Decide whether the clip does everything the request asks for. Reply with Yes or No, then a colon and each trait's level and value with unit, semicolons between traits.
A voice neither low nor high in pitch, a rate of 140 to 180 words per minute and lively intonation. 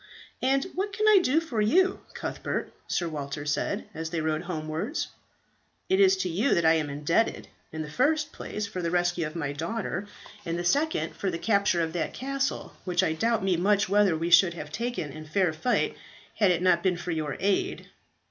No: medium, 180 Hz; fast, 205 wpm; wide, 6.3 semitones